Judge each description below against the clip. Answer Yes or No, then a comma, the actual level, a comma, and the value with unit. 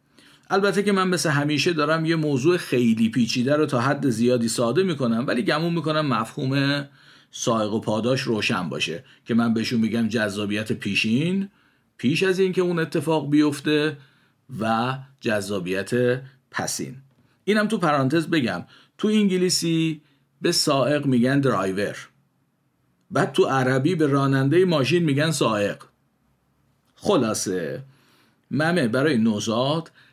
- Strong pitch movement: No, average, 4.9 semitones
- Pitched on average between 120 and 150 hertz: Yes, medium, 140 Hz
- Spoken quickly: No, average, 125 wpm